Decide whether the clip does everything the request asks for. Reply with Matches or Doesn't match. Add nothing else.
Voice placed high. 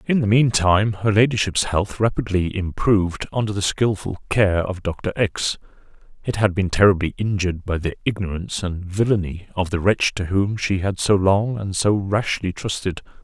Doesn't match